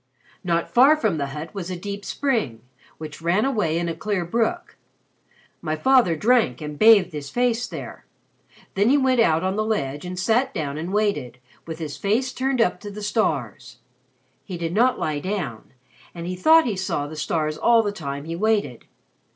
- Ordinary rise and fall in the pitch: No, wide, 6.3 semitones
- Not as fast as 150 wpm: No, average, 190 wpm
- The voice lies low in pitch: No, medium, 185 Hz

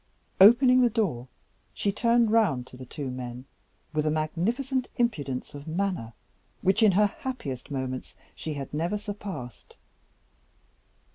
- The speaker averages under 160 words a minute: Yes, slow, 135 wpm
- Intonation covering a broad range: Yes, wide, 8.5 semitones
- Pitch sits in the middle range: Yes, medium, 175 Hz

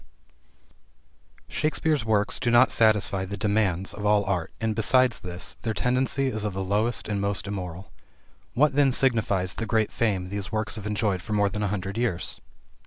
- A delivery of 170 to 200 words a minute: Yes, average, 180 wpm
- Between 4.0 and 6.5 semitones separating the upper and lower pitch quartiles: No, average, 3.0 semitones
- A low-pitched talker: Yes, low, 105 Hz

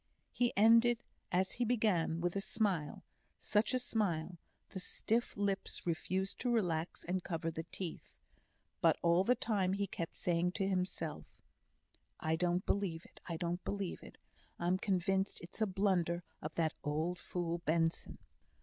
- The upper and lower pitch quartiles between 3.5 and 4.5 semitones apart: No, average, 3.1 semitones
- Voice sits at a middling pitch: Yes, medium, 180 Hz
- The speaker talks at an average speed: Yes, average, 155 wpm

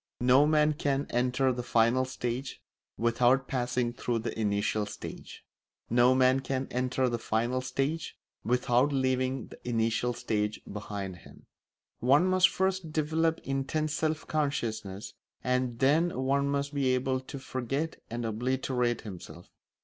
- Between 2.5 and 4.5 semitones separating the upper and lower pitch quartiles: Yes, average, 2.9 semitones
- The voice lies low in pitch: Yes, low, 130 Hz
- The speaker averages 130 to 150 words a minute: Yes, slow, 135 wpm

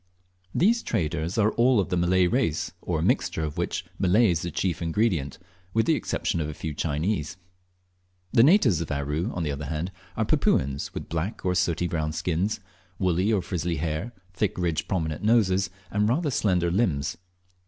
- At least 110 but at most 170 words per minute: No, average, 180 wpm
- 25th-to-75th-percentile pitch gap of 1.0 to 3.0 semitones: No, average, 4.9 semitones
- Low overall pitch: Yes, very low, 90 Hz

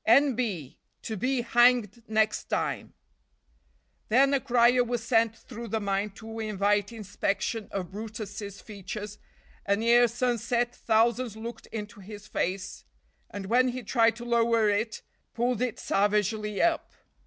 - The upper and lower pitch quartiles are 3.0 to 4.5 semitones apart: No, narrow, 2.6 semitones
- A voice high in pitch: Yes, high, 225 Hz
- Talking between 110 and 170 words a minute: Yes, average, 140 wpm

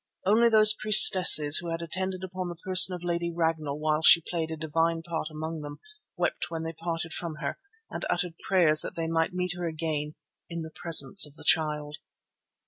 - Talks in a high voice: No, medium, 165 Hz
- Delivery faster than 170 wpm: Yes, average, 195 wpm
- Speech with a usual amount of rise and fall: No, narrow, 2.1 semitones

